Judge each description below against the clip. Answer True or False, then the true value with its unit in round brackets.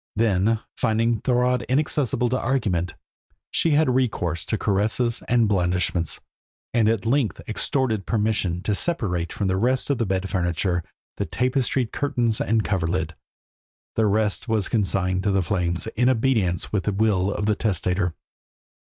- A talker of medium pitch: False (105 Hz)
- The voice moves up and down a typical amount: True (4.7 semitones)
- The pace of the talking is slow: False (150 wpm)